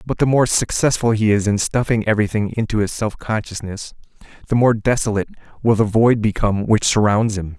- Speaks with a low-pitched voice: Yes, low, 110 Hz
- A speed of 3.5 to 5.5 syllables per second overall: No, 5.8 syllables/s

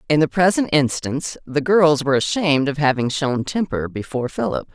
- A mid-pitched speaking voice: Yes, medium, 145 Hz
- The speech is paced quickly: No, average, 175 wpm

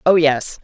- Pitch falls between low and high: Yes, medium, 155 Hz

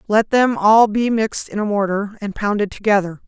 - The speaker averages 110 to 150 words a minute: No, average, 200 wpm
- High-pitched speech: Yes, high, 210 Hz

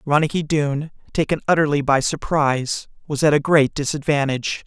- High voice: No, medium, 145 Hz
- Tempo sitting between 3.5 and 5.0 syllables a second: No, 5.6 syllables/s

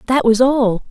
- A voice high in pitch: Yes, high, 240 Hz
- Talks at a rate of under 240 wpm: Yes, average, 200 wpm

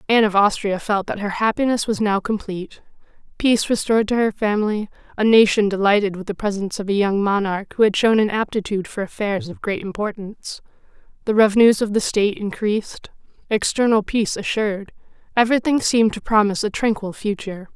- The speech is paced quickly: No, average, 170 wpm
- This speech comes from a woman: Yes, female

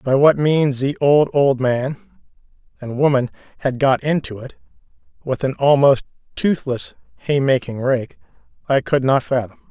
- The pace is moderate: Yes, average, 150 wpm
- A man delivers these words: Yes, male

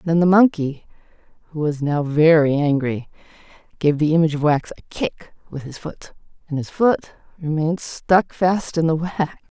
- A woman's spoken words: Yes, female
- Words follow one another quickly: No, average, 170 wpm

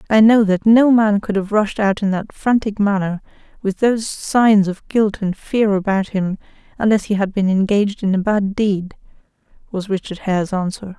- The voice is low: No, high, 205 Hz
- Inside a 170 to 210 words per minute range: Yes, average, 190 wpm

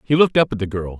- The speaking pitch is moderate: No, low, 120 Hz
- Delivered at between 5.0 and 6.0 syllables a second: No, 7.9 syllables/s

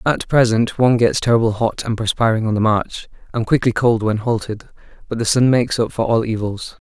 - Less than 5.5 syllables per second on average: No, 5.6 syllables/s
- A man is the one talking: Yes, male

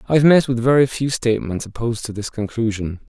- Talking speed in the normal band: No, fast, 210 wpm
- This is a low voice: Yes, low, 120 Hz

